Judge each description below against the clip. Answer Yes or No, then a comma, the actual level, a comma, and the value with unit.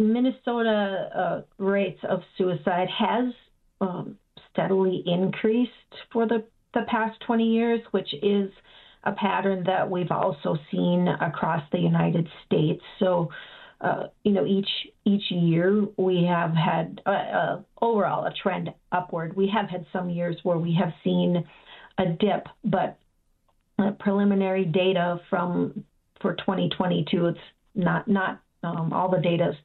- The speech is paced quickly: No, average, 140 wpm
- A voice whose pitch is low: No, high, 190 Hz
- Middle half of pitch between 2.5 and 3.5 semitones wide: Yes, average, 2.9 semitones